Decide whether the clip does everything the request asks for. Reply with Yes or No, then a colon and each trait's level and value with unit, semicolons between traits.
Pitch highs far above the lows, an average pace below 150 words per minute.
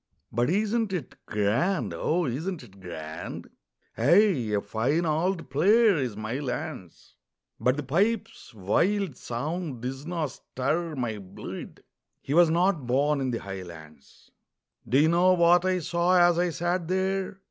Yes: wide, 7.0 semitones; average, 140 wpm